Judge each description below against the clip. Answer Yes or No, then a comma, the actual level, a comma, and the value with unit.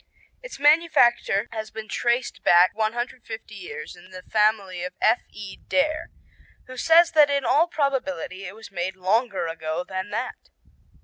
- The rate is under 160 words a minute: Yes, average, 145 wpm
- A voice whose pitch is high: Yes, high, 220 Hz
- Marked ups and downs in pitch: Yes, wide, 6.3 semitones